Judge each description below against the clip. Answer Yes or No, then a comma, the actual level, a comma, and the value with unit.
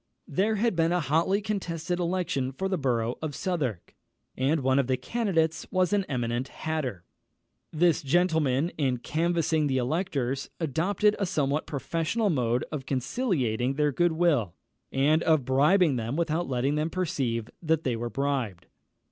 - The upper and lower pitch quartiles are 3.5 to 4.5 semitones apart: No, average, 4.9 semitones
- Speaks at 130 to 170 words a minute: Yes, average, 155 wpm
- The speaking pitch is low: No, medium, 150 Hz